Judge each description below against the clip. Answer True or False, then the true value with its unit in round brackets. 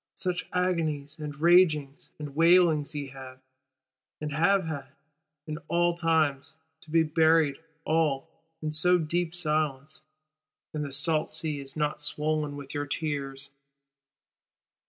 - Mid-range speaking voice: True (155 Hz)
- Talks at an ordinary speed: False (125 wpm)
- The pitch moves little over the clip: True (2.3 semitones)